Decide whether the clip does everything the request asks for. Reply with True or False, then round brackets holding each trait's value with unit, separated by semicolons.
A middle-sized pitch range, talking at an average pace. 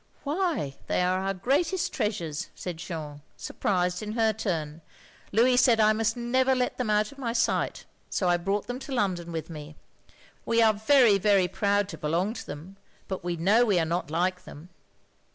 True (5.0 semitones; 190 wpm)